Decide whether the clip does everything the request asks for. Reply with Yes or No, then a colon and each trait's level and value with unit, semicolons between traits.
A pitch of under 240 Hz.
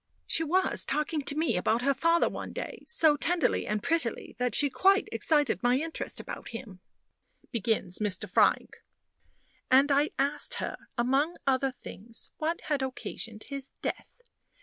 No: very high, 275 Hz